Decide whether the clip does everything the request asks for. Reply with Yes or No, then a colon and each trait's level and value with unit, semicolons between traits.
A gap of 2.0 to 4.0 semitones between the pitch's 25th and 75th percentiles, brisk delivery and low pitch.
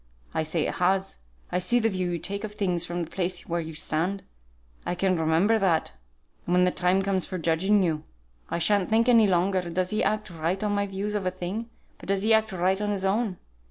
No: average, 2.7 semitones; fast, 230 wpm; high, 190 Hz